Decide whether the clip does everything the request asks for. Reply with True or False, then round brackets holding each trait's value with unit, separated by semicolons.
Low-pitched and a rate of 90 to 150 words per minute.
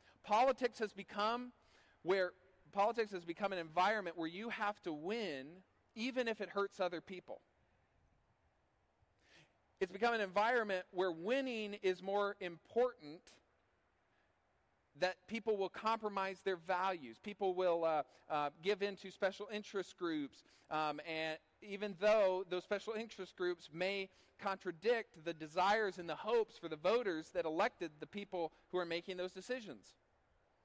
False (190 Hz; 140 wpm)